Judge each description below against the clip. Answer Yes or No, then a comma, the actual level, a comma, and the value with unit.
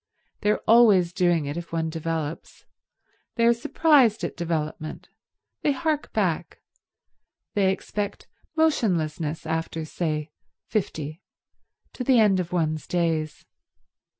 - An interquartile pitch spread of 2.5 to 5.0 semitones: No, wide, 5.4 semitones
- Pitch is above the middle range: No, medium, 175 Hz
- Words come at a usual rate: No, slow, 120 wpm